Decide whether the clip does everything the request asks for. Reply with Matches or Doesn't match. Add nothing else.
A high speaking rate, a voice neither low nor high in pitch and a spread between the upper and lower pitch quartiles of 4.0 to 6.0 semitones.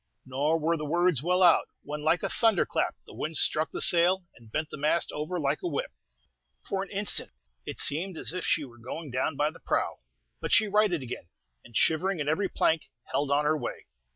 Doesn't match